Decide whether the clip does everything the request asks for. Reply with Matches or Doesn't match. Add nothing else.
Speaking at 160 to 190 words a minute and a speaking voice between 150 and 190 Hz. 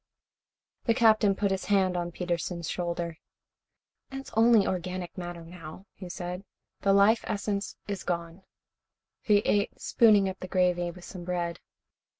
Doesn't match